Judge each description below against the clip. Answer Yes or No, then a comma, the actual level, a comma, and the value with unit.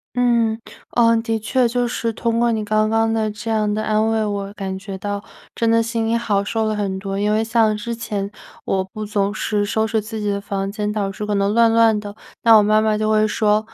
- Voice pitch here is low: No, high, 215 Hz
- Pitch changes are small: Yes, narrow, 1.6 semitones